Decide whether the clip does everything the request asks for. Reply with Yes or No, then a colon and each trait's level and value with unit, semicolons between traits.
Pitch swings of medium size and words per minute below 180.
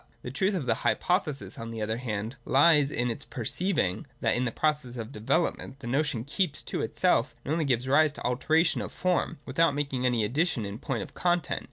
No: average, 5.0 semitones; fast, 205 wpm